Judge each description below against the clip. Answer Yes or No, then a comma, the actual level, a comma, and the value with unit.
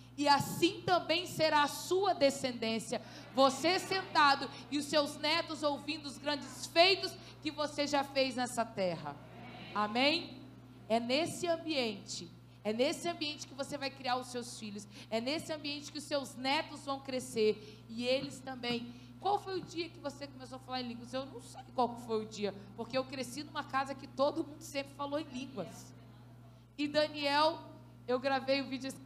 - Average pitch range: Yes, average, 3.8 semitones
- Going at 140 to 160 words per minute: No, average, 180 wpm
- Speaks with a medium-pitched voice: No, very high, 275 Hz